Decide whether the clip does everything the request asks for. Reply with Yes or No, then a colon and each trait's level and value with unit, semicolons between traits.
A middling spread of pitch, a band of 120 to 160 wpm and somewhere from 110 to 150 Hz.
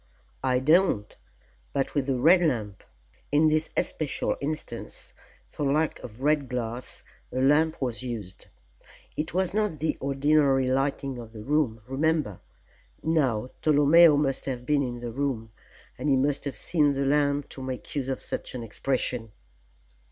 Yes: average, 3.1 semitones; average, 155 wpm; medium, 140 Hz